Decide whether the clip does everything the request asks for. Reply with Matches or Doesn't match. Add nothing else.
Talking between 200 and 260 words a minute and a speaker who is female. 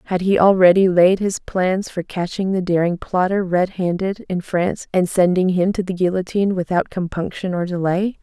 Doesn't match